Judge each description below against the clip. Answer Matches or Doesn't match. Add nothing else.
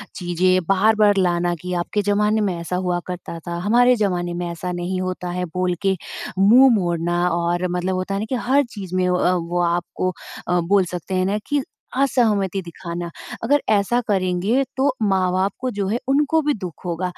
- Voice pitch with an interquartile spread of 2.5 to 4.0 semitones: Matches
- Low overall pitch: Doesn't match